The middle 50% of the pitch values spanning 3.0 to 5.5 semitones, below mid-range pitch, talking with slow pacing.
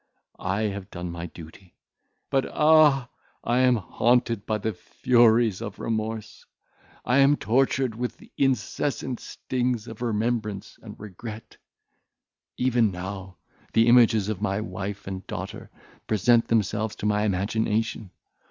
Yes: average, 3.3 semitones; low, 110 Hz; slow, 130 wpm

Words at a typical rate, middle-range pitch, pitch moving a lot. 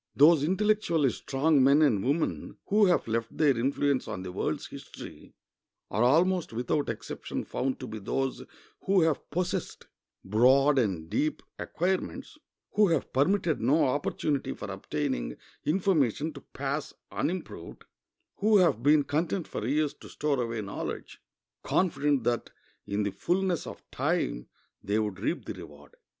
Yes: average, 145 wpm; medium, 145 Hz; wide, 6.0 semitones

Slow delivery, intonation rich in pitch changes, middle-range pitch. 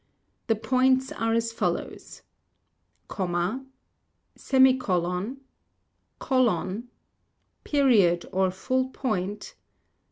No: slow, 70 wpm; wide, 5.8 semitones; high, 225 Hz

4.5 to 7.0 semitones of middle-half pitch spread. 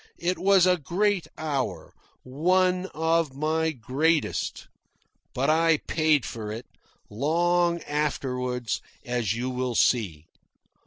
Yes: average, 5.2 semitones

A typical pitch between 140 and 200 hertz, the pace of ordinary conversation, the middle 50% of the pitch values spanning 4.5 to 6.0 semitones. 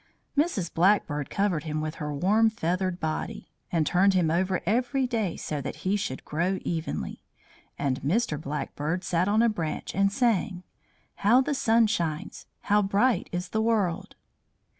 Yes: medium, 185 Hz; average, 160 wpm; average, 5.2 semitones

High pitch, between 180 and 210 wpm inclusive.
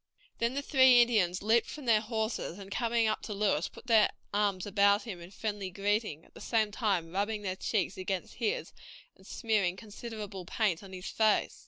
Yes: high, 210 Hz; average, 190 wpm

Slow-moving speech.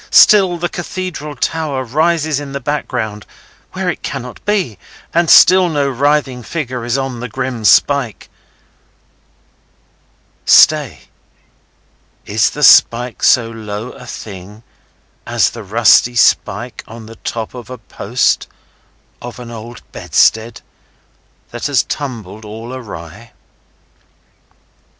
Yes: slow, 120 wpm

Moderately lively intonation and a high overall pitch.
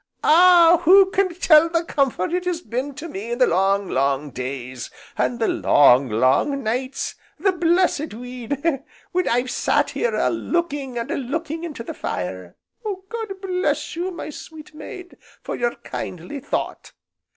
No: wide, 7.2 semitones; very high, 285 Hz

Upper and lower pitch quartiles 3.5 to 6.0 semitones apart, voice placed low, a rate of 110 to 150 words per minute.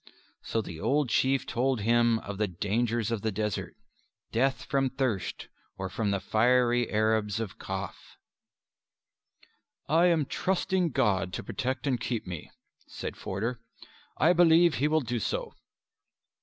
Yes: average, 4.2 semitones; low, 120 Hz; average, 140 wpm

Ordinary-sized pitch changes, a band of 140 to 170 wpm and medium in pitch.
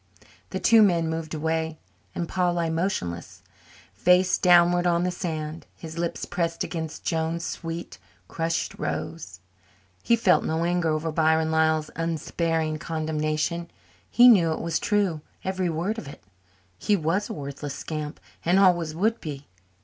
No: narrow, 2.0 semitones; average, 150 wpm; medium, 165 Hz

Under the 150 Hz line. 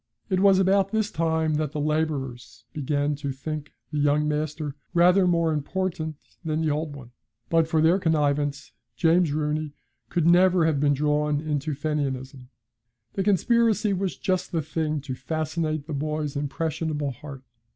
No: medium, 155 Hz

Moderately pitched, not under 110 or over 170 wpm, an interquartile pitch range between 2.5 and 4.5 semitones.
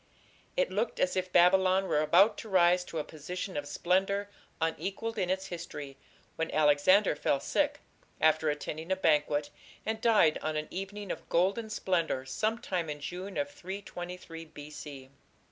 Yes: medium, 180 Hz; average, 155 wpm; average, 4.2 semitones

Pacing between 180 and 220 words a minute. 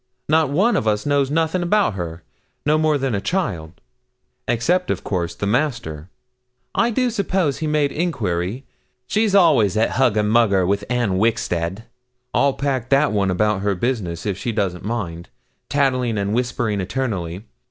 No: average, 160 wpm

